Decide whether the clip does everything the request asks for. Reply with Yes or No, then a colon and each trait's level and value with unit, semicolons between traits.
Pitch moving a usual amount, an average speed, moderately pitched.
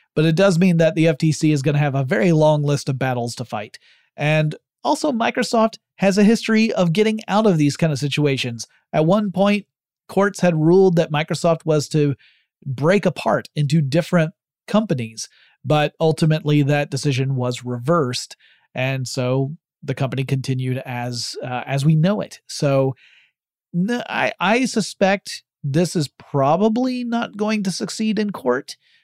No: wide, 6.2 semitones; average, 160 wpm; medium, 160 Hz